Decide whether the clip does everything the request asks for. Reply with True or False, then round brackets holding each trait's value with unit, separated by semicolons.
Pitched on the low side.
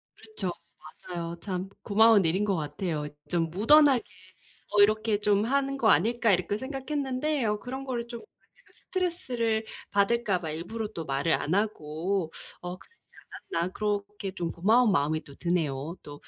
False (205 Hz)